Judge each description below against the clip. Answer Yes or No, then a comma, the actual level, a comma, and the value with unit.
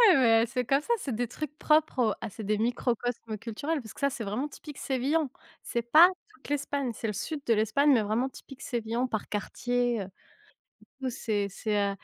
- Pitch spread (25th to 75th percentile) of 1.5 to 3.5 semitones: No, average, 4.2 semitones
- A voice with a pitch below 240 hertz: No, high, 245 Hz